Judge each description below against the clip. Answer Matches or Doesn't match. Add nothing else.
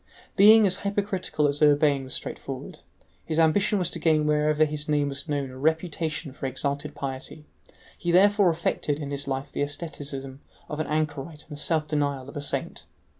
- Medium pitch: Matches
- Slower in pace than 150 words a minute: Doesn't match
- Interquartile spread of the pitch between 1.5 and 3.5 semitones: Matches